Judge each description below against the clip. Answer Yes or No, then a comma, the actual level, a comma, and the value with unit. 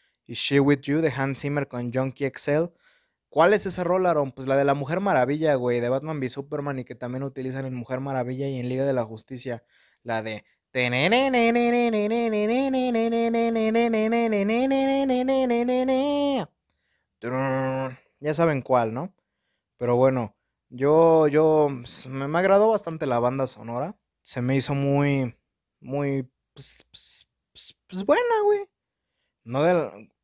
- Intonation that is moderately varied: No, wide, 9.0 semitones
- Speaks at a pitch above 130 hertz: Yes, medium, 140 Hz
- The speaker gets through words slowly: No, average, 140 wpm